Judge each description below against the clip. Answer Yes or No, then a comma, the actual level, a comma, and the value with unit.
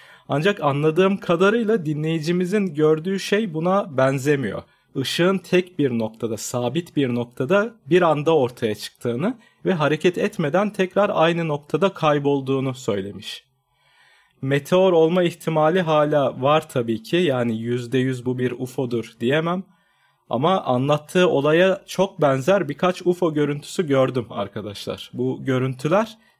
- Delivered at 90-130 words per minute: Yes, average, 120 wpm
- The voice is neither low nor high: Yes, medium, 155 Hz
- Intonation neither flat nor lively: No, wide, 5.7 semitones